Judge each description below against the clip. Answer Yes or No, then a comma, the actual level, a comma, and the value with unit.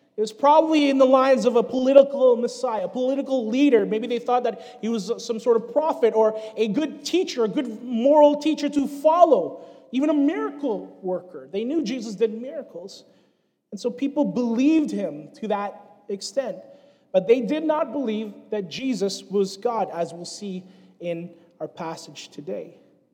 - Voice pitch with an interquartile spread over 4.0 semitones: Yes, average, 4.7 semitones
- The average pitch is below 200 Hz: No, high, 240 Hz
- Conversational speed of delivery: Yes, average, 170 wpm